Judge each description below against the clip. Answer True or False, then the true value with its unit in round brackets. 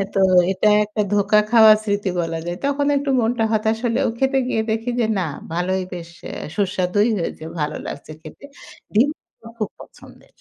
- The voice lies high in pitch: True (210 Hz)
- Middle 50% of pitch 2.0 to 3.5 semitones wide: False (3.9 semitones)